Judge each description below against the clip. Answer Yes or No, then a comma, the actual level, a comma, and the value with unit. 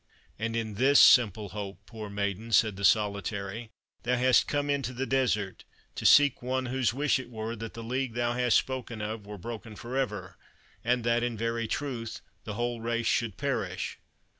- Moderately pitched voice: No, low, 115 Hz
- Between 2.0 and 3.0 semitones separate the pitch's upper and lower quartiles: Yes, average, 2.7 semitones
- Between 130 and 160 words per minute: No, average, 185 wpm